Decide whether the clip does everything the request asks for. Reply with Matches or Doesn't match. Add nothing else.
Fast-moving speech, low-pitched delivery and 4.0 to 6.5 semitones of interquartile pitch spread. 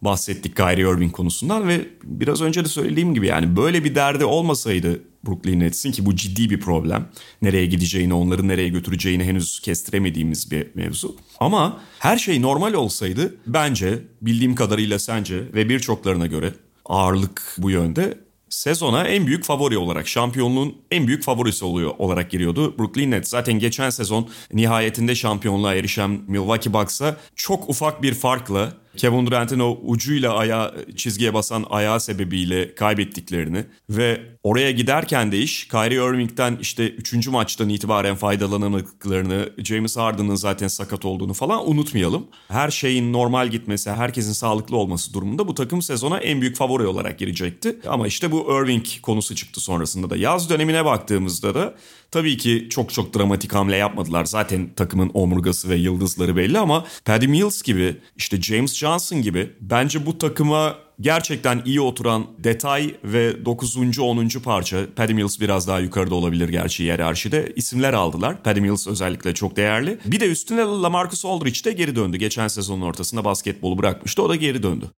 Matches